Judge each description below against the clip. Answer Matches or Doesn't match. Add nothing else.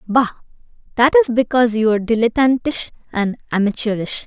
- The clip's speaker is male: Doesn't match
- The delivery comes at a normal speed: Doesn't match